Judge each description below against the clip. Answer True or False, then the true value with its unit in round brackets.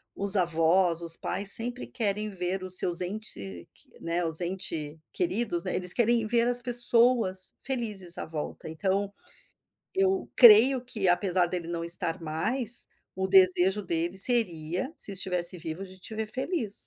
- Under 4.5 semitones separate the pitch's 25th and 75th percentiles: False (4.8 semitones)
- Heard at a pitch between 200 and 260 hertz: False (190 Hz)